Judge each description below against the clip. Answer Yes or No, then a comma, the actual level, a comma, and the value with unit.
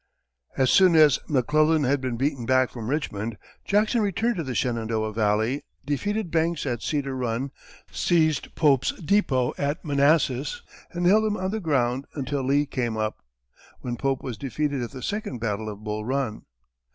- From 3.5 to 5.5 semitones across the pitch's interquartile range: Yes, average, 5.0 semitones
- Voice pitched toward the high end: No, medium, 140 Hz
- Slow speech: No, average, 165 wpm